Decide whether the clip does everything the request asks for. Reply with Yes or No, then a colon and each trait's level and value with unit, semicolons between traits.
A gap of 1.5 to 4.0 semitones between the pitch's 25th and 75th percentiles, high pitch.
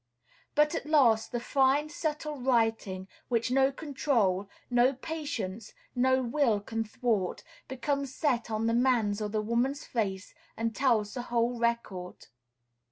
Yes: average, 3.6 semitones; high, 240 Hz